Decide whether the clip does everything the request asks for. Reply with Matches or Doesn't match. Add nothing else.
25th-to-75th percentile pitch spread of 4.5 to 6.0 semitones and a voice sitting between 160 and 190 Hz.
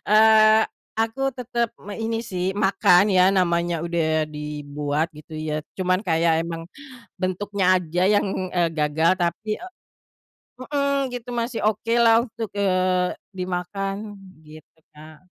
Matches